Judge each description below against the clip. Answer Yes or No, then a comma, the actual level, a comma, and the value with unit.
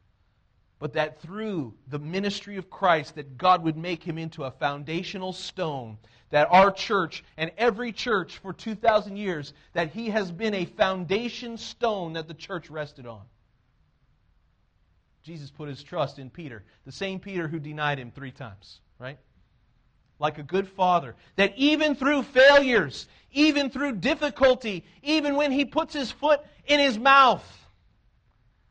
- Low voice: No, medium, 165 Hz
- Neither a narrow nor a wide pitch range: No, wide, 8.8 semitones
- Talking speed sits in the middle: Yes, average, 150 wpm